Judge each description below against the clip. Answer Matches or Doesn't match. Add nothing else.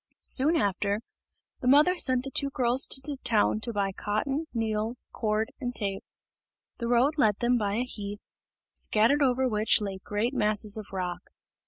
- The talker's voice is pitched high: Matches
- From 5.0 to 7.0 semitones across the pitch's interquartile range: Doesn't match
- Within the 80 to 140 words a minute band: Doesn't match